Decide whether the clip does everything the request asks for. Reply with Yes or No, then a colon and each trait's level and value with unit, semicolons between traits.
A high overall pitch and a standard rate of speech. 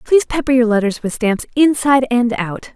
Yes: high, 245 Hz; average, 195 wpm